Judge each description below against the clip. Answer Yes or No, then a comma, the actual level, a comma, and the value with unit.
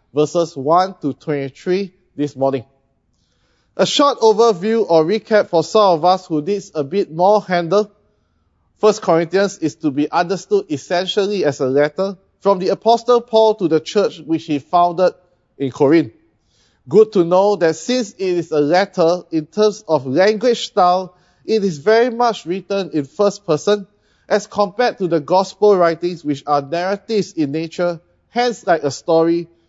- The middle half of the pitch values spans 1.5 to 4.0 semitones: No, average, 5.0 semitones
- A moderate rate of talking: Yes, average, 160 wpm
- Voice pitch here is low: No, medium, 180 Hz